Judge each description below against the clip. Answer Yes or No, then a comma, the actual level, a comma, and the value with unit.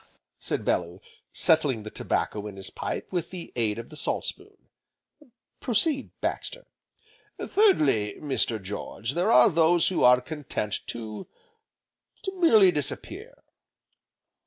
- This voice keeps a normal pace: No, slow, 125 wpm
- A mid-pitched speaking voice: Yes, medium, 150 Hz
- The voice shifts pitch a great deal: Yes, wide, 8.8 semitones